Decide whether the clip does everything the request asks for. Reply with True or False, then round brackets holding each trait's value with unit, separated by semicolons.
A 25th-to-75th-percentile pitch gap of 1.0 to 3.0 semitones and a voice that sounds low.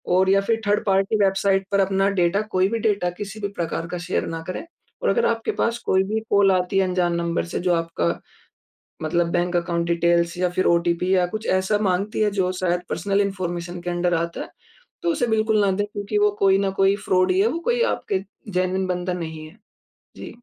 False (2.5 semitones; 185 Hz)